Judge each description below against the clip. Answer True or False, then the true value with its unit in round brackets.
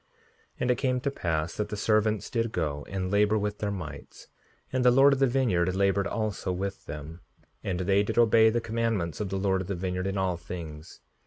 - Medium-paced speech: False (220 wpm)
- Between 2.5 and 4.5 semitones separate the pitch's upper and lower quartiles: True (3.7 semitones)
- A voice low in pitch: True (100 Hz)